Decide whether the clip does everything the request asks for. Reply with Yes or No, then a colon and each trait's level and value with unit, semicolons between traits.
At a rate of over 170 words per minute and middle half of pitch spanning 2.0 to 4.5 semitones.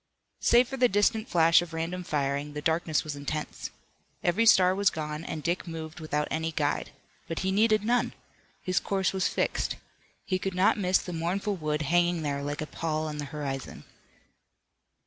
Yes: average, 180 wpm; average, 3.8 semitones